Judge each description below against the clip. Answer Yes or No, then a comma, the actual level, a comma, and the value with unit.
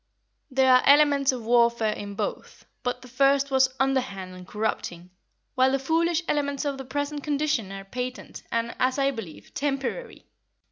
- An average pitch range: Yes, average, 3.5 semitones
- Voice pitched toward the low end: No, very high, 260 Hz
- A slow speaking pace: No, average, 160 wpm